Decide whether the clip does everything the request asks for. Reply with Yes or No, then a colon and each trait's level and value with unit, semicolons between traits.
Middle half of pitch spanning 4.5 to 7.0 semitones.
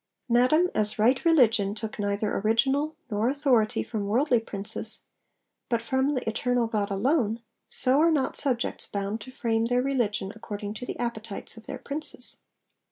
No: average, 3.7 semitones